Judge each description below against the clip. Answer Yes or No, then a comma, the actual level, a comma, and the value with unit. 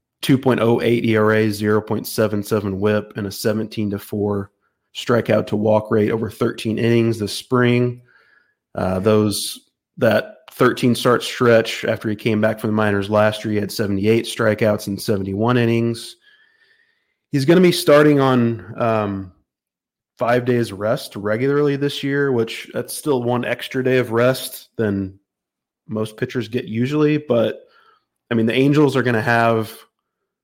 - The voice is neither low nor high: No, low, 115 Hz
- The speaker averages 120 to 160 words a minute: Yes, average, 150 wpm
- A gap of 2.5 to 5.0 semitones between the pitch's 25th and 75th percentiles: Yes, average, 2.9 semitones